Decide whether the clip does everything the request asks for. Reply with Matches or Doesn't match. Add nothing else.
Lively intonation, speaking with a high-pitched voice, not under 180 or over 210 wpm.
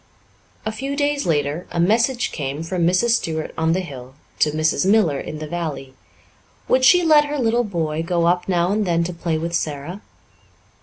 Doesn't match